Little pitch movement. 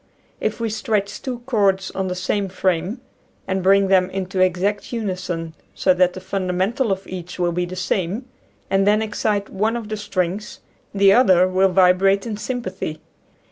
Yes: narrow, 2.3 semitones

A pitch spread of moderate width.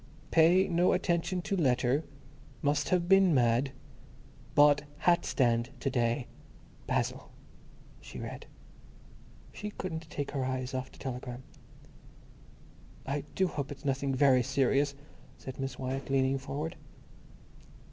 Yes: average, 3.9 semitones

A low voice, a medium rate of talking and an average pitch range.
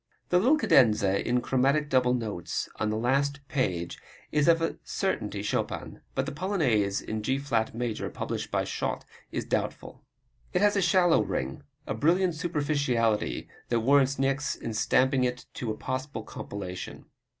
Yes: low, 130 Hz; average, 160 wpm; average, 5.0 semitones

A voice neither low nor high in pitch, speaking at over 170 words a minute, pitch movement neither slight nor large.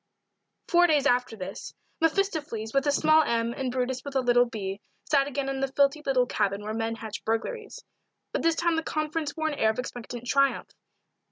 No: very high, 270 Hz; average, 195 wpm; average, 5.0 semitones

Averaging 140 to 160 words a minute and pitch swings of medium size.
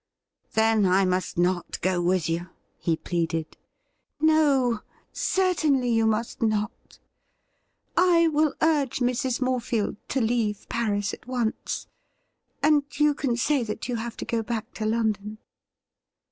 Yes: average, 145 wpm; average, 4.7 semitones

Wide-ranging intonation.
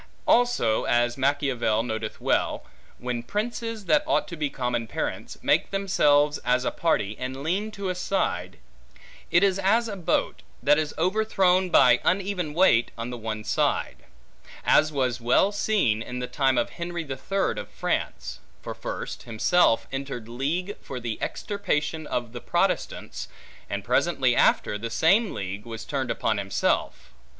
Yes: wide, 7.8 semitones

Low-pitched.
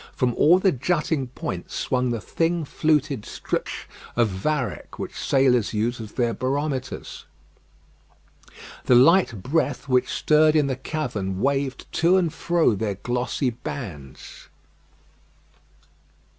Yes: low, 130 Hz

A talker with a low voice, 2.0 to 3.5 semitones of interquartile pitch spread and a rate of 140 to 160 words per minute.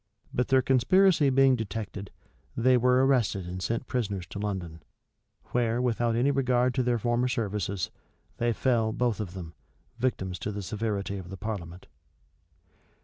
No: low, 115 Hz; average, 4.1 semitones; average, 150 wpm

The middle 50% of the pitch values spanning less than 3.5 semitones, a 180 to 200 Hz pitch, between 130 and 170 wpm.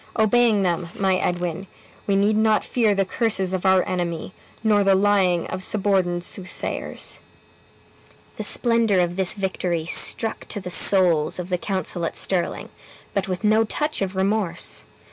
Yes: narrow, 2.6 semitones; high, 190 Hz; average, 155 wpm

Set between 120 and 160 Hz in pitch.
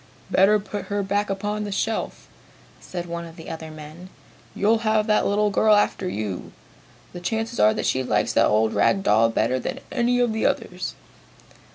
No: high, 195 Hz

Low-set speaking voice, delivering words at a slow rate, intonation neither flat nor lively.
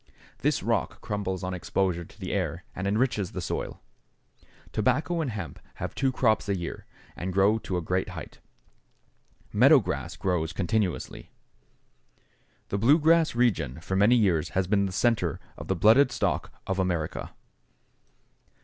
No: low, 100 Hz; average, 150 wpm; average, 4.2 semitones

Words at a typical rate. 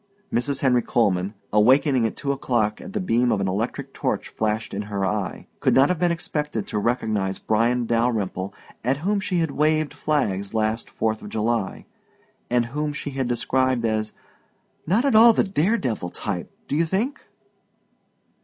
Yes: average, 170 wpm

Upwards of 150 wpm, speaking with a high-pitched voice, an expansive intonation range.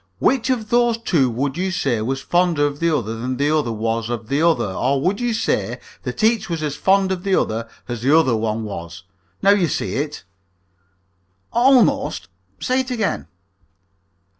No: average, 185 wpm; medium, 150 Hz; wide, 8.7 semitones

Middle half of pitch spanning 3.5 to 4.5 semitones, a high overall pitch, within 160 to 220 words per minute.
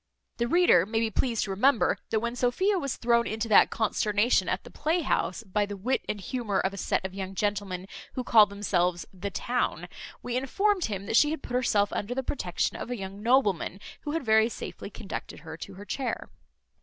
Yes: average, 4.1 semitones; high, 220 Hz; fast, 205 wpm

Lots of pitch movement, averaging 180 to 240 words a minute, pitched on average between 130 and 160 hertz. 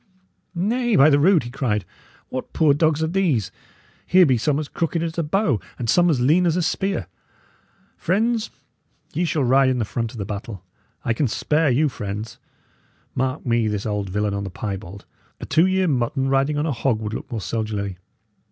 Yes: wide, 6.9 semitones; average, 200 wpm; low, 135 Hz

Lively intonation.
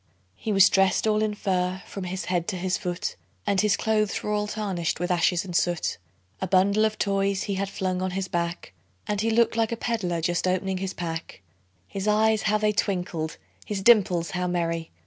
No: average, 2.9 semitones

